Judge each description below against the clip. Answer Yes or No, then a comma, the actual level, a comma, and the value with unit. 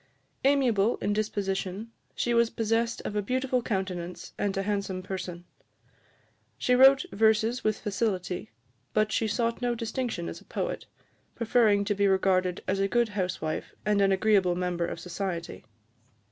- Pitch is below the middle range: No, high, 205 Hz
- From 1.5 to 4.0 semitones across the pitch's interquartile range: Yes, average, 3.4 semitones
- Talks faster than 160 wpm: No, average, 150 wpm